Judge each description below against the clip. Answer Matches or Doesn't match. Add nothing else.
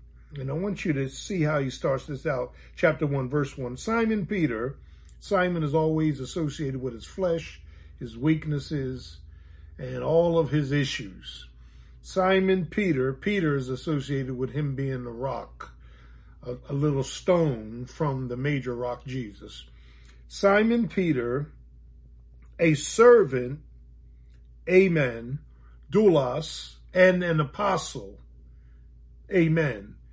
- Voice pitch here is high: Doesn't match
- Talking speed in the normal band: Doesn't match